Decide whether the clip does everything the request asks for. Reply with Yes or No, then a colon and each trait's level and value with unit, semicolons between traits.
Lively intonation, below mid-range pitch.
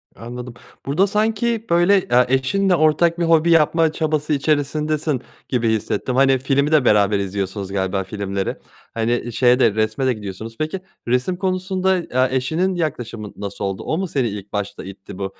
Yes: wide, 7.2 semitones; low, 130 Hz